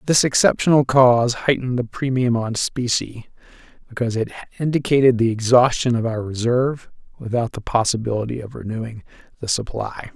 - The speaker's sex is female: No, male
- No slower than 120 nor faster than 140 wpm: Yes, slow, 135 wpm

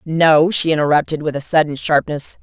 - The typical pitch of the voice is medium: Yes, medium, 155 Hz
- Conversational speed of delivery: Yes, average, 175 wpm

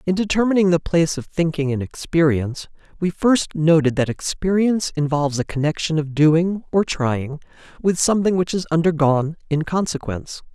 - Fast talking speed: No, average, 155 wpm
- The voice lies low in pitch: No, medium, 165 Hz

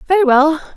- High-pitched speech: Yes, very high, 285 Hz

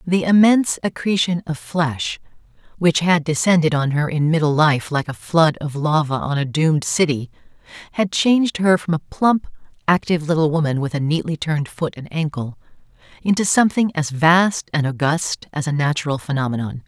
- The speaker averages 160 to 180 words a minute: Yes, average, 170 wpm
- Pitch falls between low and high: Yes, medium, 155 Hz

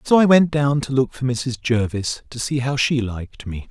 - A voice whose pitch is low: Yes, low, 130 Hz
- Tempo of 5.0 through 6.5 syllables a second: No, 4.8 syllables/s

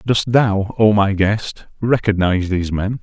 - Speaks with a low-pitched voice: Yes, low, 105 Hz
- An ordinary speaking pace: Yes, average, 160 wpm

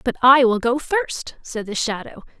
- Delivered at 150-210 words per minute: Yes, average, 200 wpm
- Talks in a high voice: Yes, very high, 250 Hz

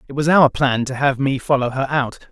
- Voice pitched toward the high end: No, low, 135 Hz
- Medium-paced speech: No, fast, 260 wpm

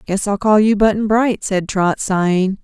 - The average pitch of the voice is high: Yes, high, 200 Hz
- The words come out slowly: No, fast, 205 wpm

